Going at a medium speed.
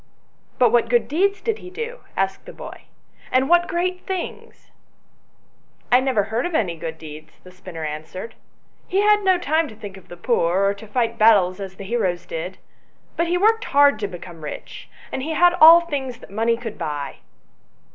No: fast, 210 wpm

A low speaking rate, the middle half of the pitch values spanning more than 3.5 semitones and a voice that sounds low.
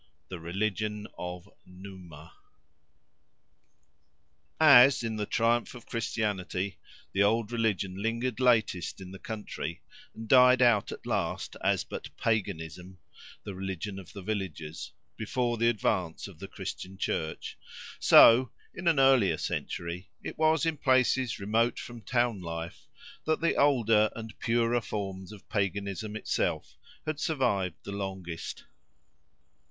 Yes: slow, 125 wpm; average, 4.1 semitones; low, 105 Hz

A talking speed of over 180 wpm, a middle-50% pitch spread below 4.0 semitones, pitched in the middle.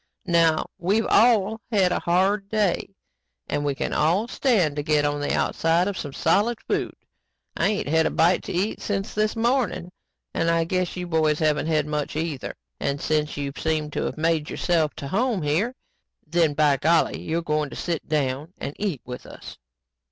No: average, 190 wpm; average, 4.4 semitones; medium, 165 Hz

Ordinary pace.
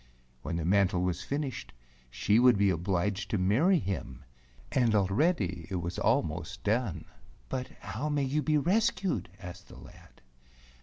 Yes: average, 160 wpm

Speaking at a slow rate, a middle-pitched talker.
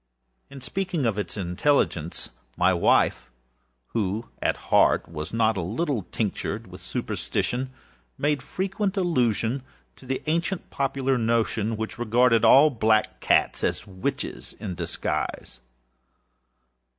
No: slow, 120 wpm; low, 115 Hz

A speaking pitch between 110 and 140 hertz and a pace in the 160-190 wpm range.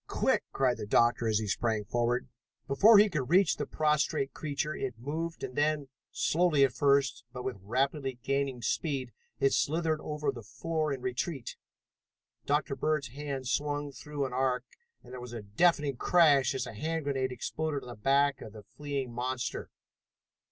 Yes: low, 135 Hz; average, 175 wpm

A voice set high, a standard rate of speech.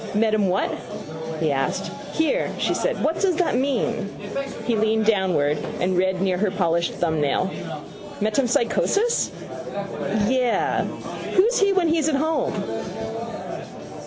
No: high, 220 Hz; slow, 125 wpm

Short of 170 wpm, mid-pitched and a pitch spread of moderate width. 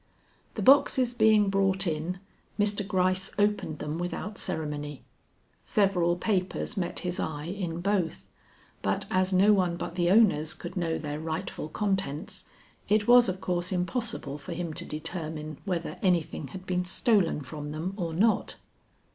Yes: average, 150 wpm; medium, 180 Hz; average, 3.6 semitones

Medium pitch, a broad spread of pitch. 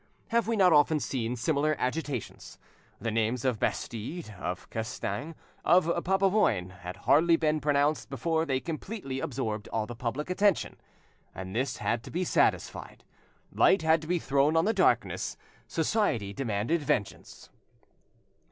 Yes: medium, 145 Hz; wide, 6.1 semitones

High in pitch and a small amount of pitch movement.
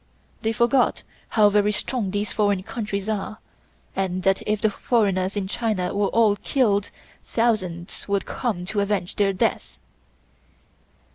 Yes: high, 205 Hz; narrow, 2.1 semitones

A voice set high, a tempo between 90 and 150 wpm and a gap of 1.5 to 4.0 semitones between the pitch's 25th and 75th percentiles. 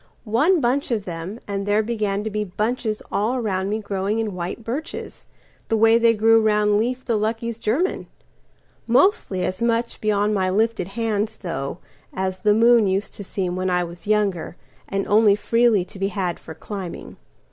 No: high, 210 Hz; average, 160 wpm; average, 2.9 semitones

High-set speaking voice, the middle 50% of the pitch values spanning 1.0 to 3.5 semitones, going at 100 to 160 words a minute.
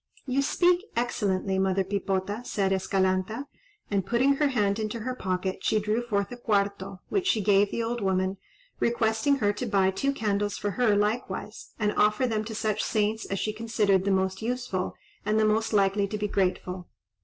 No: high, 210 Hz; average, 3.0 semitones; average, 185 wpm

